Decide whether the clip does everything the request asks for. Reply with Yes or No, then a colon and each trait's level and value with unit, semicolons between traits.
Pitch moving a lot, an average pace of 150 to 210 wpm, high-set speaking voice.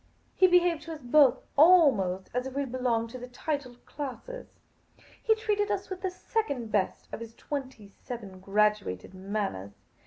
Yes: wide, 7.7 semitones; average, 160 wpm; very high, 255 Hz